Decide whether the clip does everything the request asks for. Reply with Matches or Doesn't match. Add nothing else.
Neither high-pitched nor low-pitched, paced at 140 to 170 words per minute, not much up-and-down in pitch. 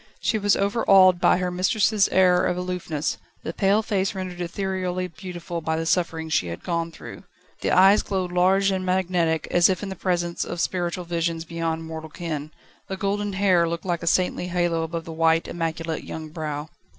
Doesn't match